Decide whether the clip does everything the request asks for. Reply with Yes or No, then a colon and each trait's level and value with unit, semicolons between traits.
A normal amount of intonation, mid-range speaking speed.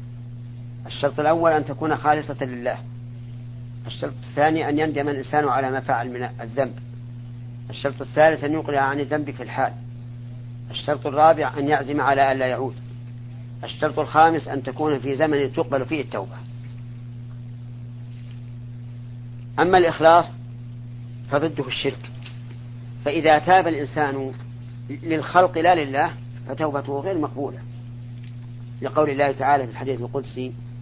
Yes: average, 3.3 semitones; average, 115 wpm